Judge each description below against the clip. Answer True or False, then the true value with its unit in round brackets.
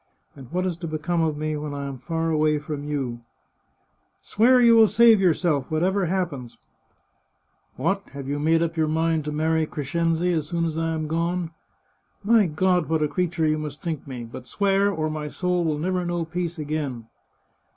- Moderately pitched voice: True (160 Hz)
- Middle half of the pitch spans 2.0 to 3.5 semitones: True (2.9 semitones)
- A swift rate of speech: True (215 wpm)